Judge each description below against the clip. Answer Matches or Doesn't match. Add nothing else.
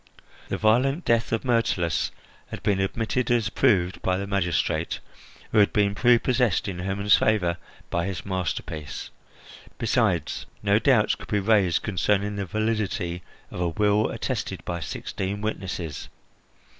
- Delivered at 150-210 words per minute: Doesn't match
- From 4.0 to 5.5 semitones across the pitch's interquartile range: Doesn't match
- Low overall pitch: Matches